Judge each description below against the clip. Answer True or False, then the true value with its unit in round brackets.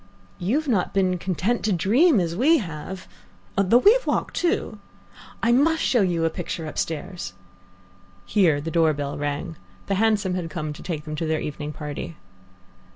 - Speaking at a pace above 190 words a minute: False (185 wpm)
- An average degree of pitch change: False (5.8 semitones)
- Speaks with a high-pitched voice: False (175 Hz)